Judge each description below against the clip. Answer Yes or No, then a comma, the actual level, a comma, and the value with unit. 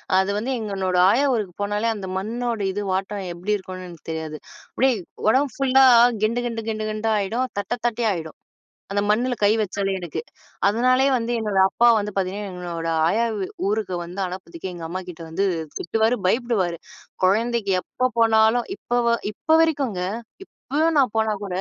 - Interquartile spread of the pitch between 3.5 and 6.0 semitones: Yes, average, 4.1 semitones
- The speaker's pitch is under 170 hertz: No, high, 210 Hz